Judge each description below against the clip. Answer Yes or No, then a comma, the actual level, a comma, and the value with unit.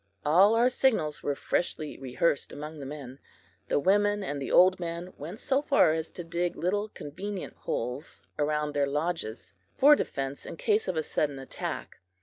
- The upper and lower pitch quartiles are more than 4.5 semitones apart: Yes, average, 5.2 semitones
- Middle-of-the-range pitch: Yes, medium, 165 Hz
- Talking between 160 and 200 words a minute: Yes, average, 165 wpm